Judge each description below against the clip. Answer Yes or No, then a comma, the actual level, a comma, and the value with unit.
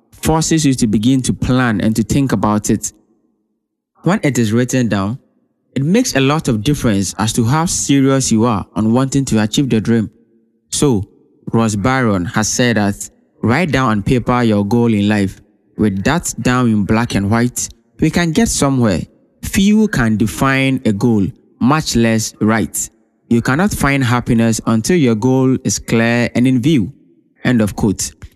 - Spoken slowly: No, average, 175 wpm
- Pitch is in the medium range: No, low, 115 Hz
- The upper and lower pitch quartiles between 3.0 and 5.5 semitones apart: Yes, average, 3.4 semitones